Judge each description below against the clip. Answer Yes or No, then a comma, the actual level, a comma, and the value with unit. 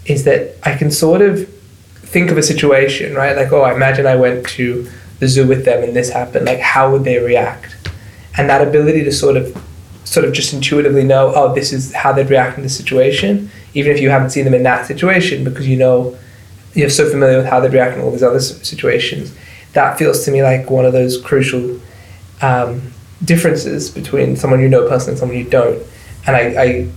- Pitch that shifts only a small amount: Yes, narrow, 2.2 semitones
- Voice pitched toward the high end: No, low, 130 Hz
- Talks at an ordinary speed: No, fast, 220 wpm